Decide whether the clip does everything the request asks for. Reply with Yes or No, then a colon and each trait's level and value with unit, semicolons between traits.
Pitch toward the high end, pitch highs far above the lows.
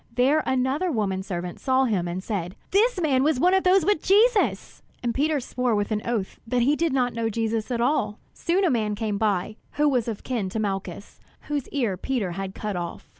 Yes: high, 235 Hz; wide, 6.1 semitones